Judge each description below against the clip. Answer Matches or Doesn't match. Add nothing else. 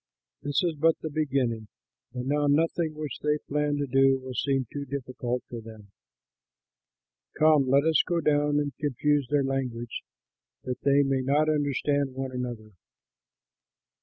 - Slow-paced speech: Doesn't match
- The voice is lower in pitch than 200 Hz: Matches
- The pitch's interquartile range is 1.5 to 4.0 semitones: Matches